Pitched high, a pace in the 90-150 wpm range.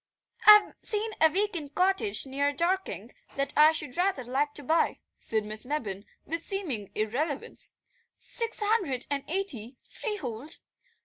Yes: very high, 300 Hz; average, 140 wpm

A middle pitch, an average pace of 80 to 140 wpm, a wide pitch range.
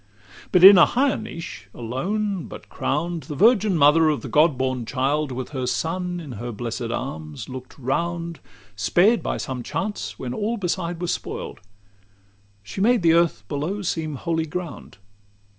No: medium, 160 Hz; average, 165 wpm; wide, 5.7 semitones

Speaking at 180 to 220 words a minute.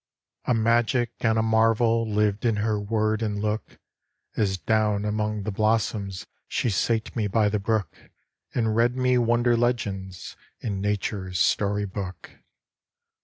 No: average, 140 wpm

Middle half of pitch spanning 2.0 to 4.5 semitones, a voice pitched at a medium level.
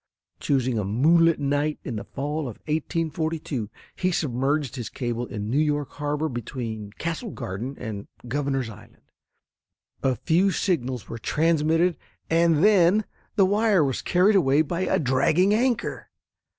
No: average, 5.2 semitones; medium, 145 Hz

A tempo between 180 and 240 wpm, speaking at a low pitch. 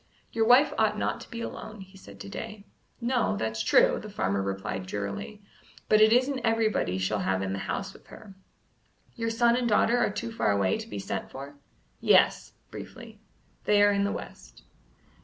No: average, 190 wpm; high, 205 Hz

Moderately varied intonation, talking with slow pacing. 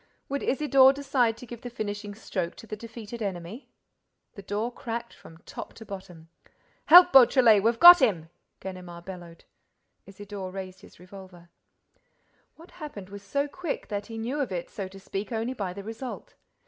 No: average, 4.6 semitones; average, 170 wpm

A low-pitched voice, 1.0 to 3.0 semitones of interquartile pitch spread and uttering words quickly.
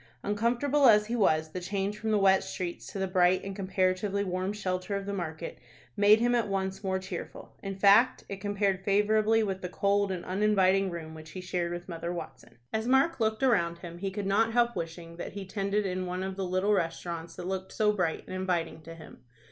No: high, 195 Hz; narrow, 2.5 semitones; fast, 215 wpm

